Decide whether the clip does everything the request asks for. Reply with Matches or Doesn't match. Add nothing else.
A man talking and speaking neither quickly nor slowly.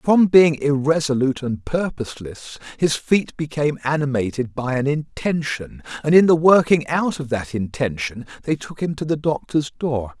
Matches